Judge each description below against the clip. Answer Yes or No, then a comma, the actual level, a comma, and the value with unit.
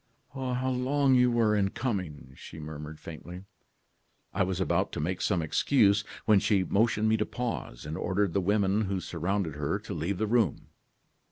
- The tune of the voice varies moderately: Yes, average, 4.6 semitones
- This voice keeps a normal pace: Yes, average, 175 wpm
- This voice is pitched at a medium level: No, low, 100 Hz